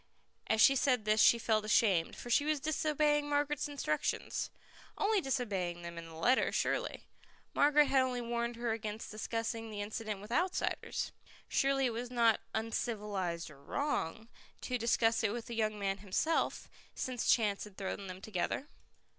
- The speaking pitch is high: Yes, high, 225 Hz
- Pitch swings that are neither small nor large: Yes, average, 4.4 semitones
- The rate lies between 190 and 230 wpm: No, average, 165 wpm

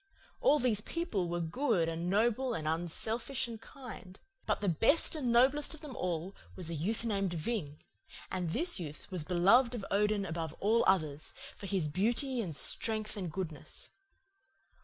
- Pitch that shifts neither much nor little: No, wide, 5.8 semitones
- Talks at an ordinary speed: Yes, average, 165 wpm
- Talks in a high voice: Yes, high, 200 Hz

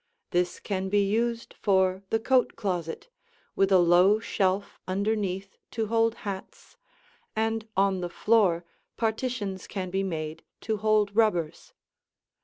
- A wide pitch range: No, average, 2.9 semitones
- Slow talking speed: Yes, slow, 130 wpm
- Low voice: No, high, 200 Hz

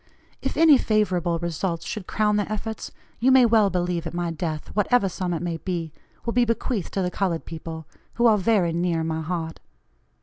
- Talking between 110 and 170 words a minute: No, average, 195 wpm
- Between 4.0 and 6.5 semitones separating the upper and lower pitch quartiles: Yes, average, 4.3 semitones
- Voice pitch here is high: No, medium, 180 Hz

